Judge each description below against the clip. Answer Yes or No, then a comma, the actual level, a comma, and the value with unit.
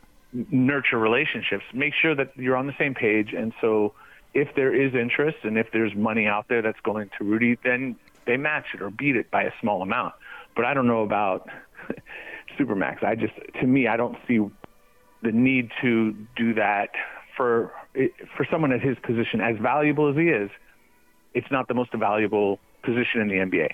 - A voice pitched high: No, low, 120 Hz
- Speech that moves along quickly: No, average, 190 wpm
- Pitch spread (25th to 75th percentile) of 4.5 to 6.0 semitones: No, average, 3.2 semitones